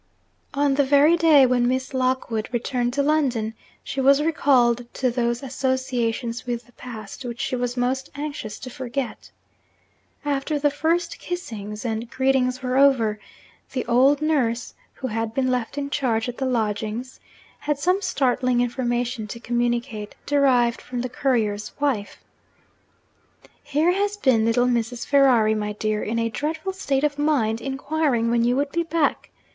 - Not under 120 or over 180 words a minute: Yes, average, 155 wpm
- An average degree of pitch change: Yes, average, 3.1 semitones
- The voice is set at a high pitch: Yes, very high, 255 Hz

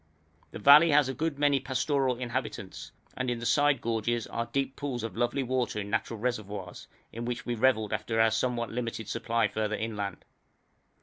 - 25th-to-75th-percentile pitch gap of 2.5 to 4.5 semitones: Yes, average, 2.9 semitones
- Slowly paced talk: No, average, 180 wpm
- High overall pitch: No, low, 120 Hz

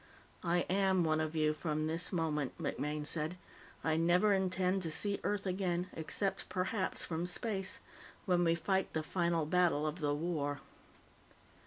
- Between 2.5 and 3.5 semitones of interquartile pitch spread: Yes, average, 3.0 semitones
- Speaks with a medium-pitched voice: Yes, medium, 175 Hz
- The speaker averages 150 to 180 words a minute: Yes, average, 155 wpm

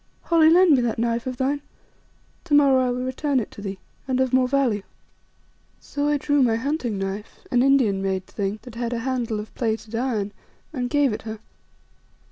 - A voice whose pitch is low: No, very high, 250 Hz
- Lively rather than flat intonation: No, average, 3.9 semitones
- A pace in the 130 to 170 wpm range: No, average, 195 wpm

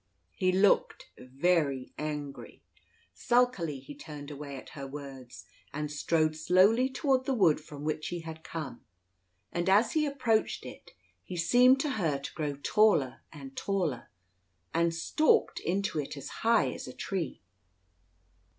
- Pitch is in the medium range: Yes, medium, 165 Hz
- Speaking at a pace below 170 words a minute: Yes, average, 145 wpm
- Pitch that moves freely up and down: Yes, wide, 6.2 semitones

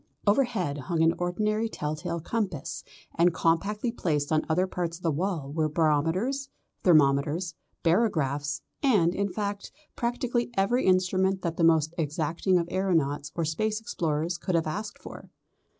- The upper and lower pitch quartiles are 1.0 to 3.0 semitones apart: No, average, 4.3 semitones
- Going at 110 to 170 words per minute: Yes, average, 150 wpm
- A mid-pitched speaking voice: Yes, medium, 175 Hz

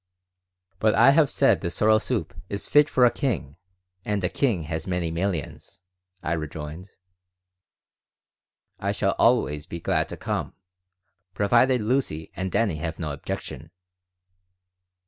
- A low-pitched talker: Yes, very low, 95 Hz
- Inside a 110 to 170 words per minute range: Yes, slow, 135 wpm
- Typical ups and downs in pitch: No, wide, 6.4 semitones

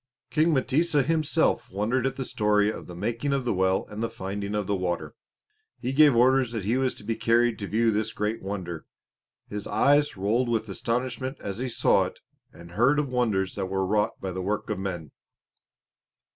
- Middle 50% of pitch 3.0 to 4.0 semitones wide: No, average, 4.5 semitones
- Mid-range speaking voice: No, low, 110 Hz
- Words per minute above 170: Yes, average, 200 wpm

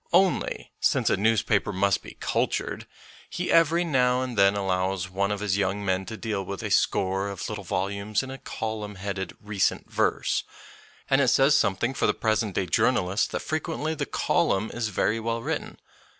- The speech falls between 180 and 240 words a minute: Yes, average, 190 wpm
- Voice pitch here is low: Yes, low, 105 Hz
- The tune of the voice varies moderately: Yes, average, 3.8 semitones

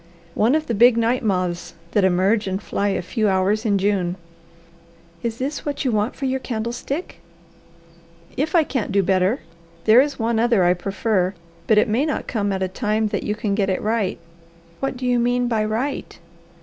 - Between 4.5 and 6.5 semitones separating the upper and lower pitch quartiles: No, average, 3.9 semitones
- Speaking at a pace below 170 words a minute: No, average, 195 wpm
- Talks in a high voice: Yes, high, 220 Hz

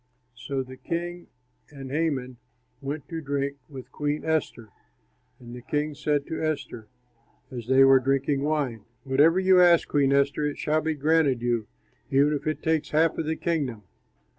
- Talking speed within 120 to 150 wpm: No, average, 165 wpm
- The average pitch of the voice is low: No, medium, 145 Hz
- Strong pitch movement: No, average, 2.9 semitones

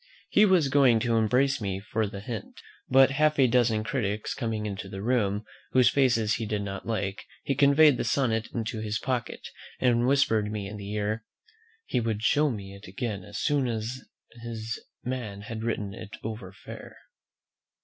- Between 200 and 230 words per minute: No, average, 180 wpm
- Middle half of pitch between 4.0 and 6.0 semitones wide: No, average, 3.4 semitones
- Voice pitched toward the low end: Yes, low, 110 Hz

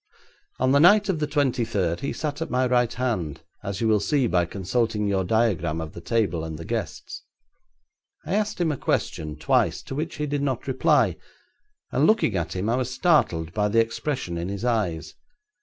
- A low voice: Yes, low, 115 Hz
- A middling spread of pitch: No, wide, 7.4 semitones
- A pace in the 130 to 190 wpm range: No, average, 200 wpm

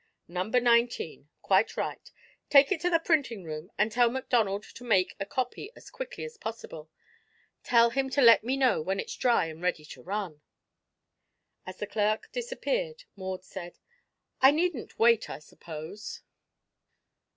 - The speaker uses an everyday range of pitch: No, wide, 6.3 semitones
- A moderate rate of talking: Yes, average, 160 wpm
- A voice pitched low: No, high, 230 Hz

